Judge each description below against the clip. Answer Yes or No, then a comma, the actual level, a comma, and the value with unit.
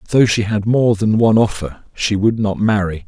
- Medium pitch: No, low, 105 Hz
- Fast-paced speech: Yes, fast, 215 wpm